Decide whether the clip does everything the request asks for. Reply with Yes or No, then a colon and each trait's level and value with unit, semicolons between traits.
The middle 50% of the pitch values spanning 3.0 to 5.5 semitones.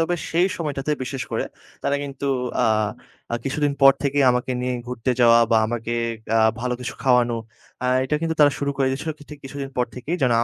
No: narrow, 2.6 semitones